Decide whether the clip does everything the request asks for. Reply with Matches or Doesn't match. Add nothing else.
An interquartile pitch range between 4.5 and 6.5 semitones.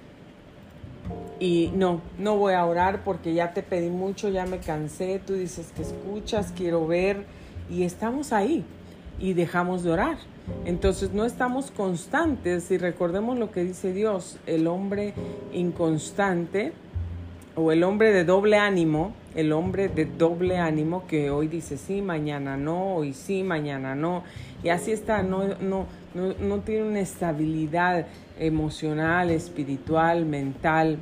Doesn't match